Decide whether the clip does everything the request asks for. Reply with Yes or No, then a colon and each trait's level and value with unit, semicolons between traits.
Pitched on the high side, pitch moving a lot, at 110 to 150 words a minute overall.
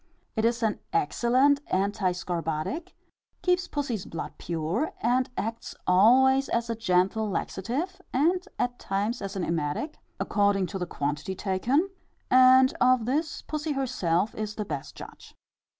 Yes: high, 225 Hz; wide, 5.9 semitones; average, 140 wpm